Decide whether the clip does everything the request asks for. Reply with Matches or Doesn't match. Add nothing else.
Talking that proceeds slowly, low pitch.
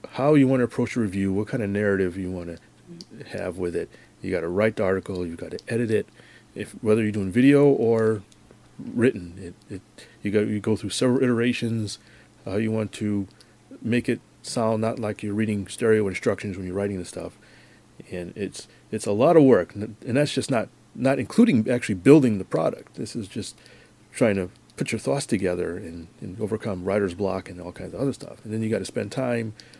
Doesn't match